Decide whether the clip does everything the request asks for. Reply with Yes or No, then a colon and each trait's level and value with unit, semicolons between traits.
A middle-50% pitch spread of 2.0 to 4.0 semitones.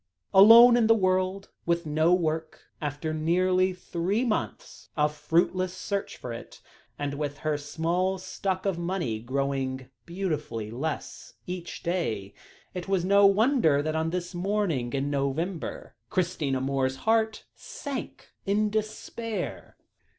No: average, 5.0 semitones